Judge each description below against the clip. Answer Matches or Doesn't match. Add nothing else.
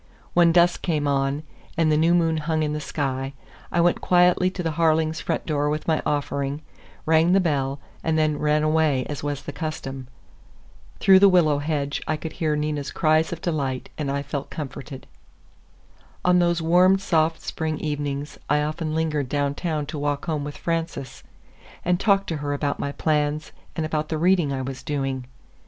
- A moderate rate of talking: Matches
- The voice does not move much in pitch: Matches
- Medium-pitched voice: Matches